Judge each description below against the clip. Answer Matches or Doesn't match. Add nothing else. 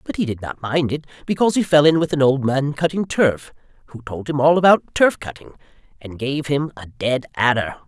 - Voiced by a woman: Doesn't match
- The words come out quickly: Matches